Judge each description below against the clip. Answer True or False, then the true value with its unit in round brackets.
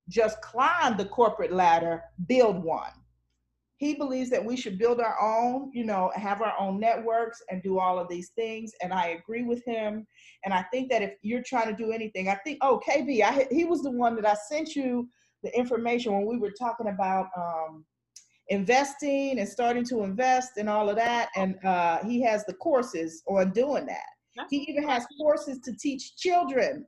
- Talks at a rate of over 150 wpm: True (195 wpm)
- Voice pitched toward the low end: False (230 Hz)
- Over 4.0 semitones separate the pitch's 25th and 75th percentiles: True (5.0 semitones)